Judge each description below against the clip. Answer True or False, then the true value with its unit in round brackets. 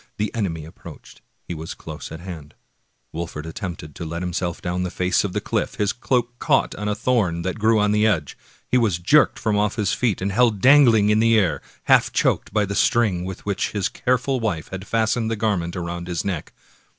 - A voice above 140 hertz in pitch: False (100 Hz)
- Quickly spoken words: True (215 wpm)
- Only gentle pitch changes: False (4.3 semitones)